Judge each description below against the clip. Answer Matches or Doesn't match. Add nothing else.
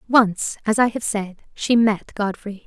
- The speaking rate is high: Doesn't match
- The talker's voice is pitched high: Matches